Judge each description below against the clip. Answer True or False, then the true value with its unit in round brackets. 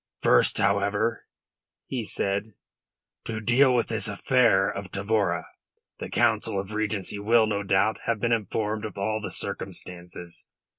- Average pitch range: False (2.0 semitones)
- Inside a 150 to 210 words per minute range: False (140 wpm)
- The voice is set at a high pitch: False (105 Hz)